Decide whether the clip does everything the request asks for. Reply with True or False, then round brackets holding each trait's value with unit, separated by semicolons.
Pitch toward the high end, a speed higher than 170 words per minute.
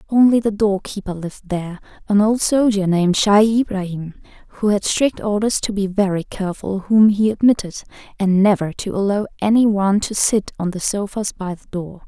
True (200 Hz; 185 wpm)